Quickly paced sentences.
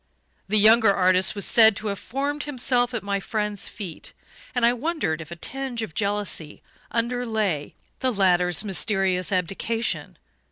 No: average, 150 wpm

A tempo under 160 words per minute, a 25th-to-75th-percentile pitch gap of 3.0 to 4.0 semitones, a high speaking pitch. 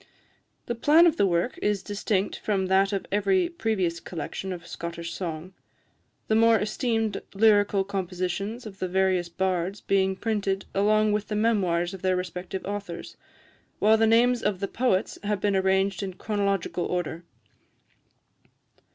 No: average, 150 wpm; narrow, 2.5 semitones; high, 195 Hz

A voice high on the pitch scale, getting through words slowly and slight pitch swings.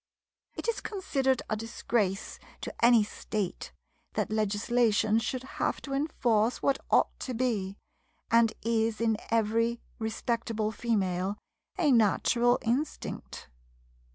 Yes: high, 230 Hz; slow, 115 wpm; narrow, 2.3 semitones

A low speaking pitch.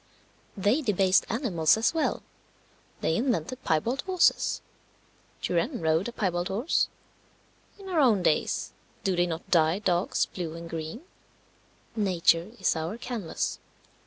No: high, 190 Hz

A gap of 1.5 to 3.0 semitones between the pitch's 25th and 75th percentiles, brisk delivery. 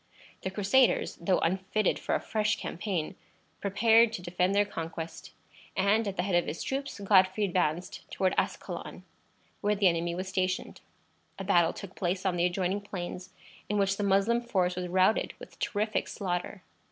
No: narrow, 2.4 semitones; average, 165 wpm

